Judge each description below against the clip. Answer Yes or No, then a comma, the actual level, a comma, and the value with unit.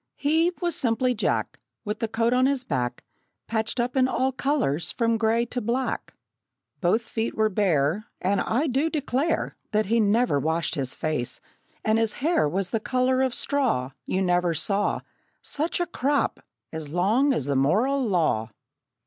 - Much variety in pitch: Yes, wide, 6.6 semitones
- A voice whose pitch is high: Yes, high, 225 Hz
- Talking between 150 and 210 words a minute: Yes, average, 165 wpm